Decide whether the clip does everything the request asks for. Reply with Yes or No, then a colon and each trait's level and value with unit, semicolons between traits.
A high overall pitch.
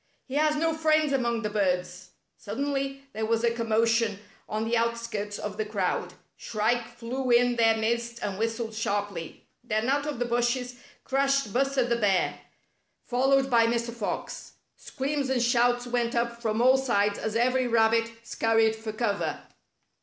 Yes: high, 235 Hz